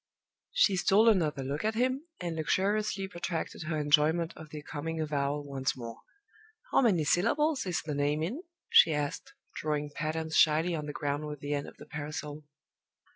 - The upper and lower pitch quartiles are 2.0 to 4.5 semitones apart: Yes, average, 3.9 semitones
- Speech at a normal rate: Yes, average, 175 wpm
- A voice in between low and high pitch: Yes, medium, 155 Hz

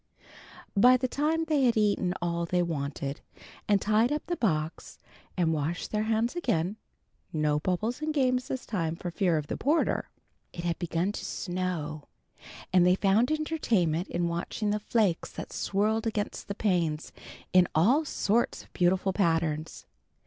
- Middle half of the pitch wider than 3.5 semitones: Yes, wide, 5.4 semitones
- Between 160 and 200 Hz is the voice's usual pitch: Yes, high, 190 Hz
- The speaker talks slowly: No, average, 160 wpm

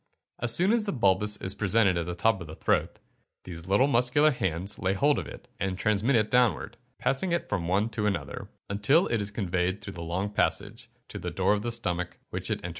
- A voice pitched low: Yes, low, 105 Hz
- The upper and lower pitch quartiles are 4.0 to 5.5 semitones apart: Yes, average, 4.4 semitones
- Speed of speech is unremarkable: No, fast, 225 wpm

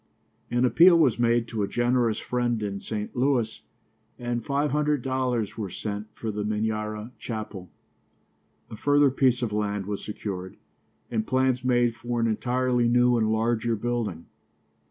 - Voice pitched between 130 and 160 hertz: No, low, 120 Hz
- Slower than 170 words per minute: Yes, average, 155 wpm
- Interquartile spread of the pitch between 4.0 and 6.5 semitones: No, average, 2.7 semitones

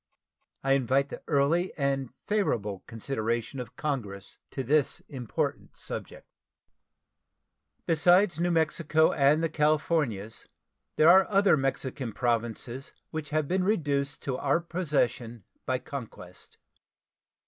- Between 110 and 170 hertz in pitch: Yes, medium, 140 Hz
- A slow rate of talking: Yes, slow, 115 wpm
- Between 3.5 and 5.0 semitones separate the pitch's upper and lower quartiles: Yes, average, 4.6 semitones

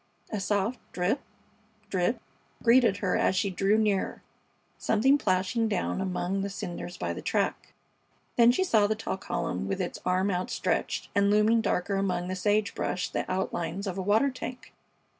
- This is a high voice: Yes, high, 200 Hz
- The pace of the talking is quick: No, average, 165 wpm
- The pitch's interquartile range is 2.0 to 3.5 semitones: Yes, average, 3.1 semitones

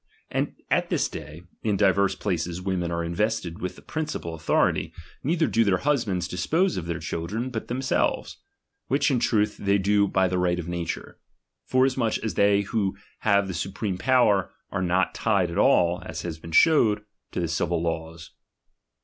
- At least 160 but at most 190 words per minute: Yes, average, 175 wpm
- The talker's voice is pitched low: Yes, very low, 95 Hz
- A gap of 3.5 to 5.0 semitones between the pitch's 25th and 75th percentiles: Yes, average, 4.3 semitones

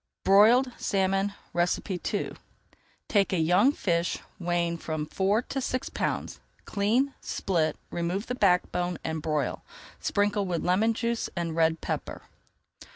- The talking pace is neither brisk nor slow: No, slow, 125 wpm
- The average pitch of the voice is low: No, high, 190 Hz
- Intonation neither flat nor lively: Yes, average, 3.6 semitones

